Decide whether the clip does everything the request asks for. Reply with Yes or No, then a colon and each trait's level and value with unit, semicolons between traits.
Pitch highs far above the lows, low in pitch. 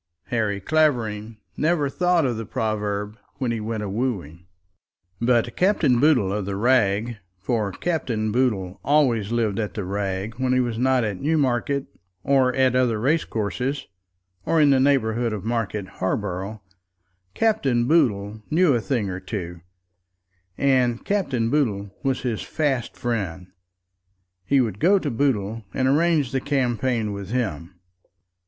No: average, 4.6 semitones; low, 120 Hz